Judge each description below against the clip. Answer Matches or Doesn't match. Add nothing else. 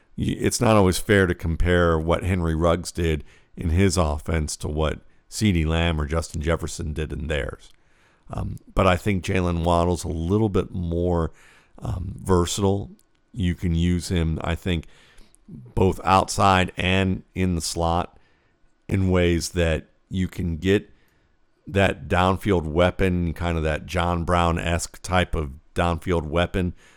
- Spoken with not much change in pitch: Matches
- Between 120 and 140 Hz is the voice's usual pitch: Doesn't match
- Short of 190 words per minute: Matches